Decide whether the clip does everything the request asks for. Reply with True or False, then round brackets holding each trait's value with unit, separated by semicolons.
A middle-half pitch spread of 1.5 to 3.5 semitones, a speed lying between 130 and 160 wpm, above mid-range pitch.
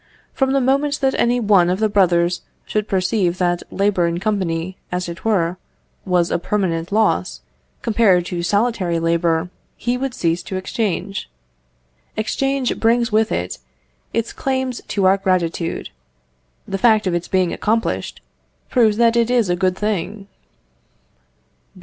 False (4.4 semitones; 145 wpm; 195 Hz)